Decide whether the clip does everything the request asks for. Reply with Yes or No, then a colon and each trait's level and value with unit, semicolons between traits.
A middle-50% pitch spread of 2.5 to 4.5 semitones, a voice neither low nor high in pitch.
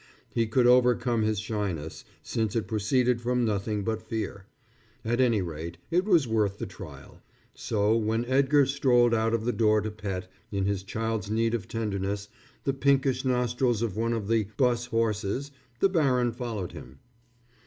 No: average, 3.0 semitones; low, 115 Hz